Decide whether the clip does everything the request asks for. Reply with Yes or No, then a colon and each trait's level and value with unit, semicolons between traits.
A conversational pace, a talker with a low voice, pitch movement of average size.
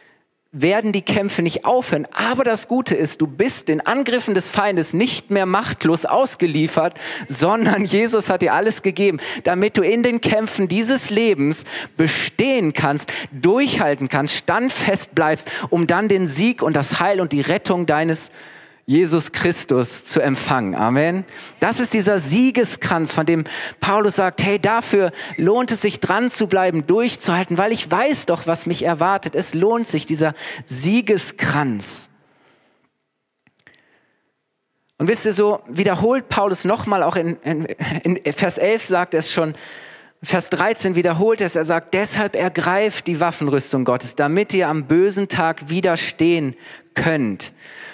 No: average, 145 wpm; medium, 180 Hz; average, 4.6 semitones